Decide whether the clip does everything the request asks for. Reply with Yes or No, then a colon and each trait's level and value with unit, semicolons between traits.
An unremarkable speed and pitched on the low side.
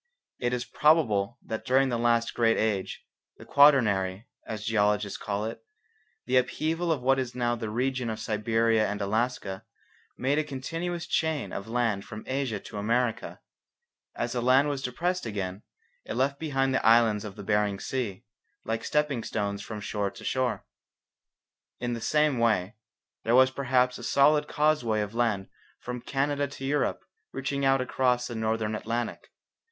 Yes: average, 165 wpm; low, 120 Hz